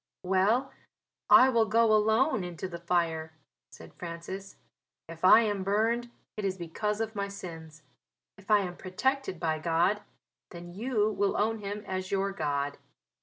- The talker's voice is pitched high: Yes, high, 195 Hz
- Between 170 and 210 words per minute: No, average, 155 wpm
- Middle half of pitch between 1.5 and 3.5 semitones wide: No, average, 3.9 semitones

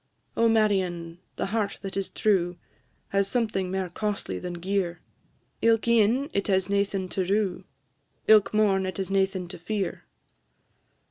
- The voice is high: Yes, high, 195 Hz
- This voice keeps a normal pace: Yes, average, 145 wpm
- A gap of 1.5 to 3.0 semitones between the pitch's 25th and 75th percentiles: Yes, narrow, 2.4 semitones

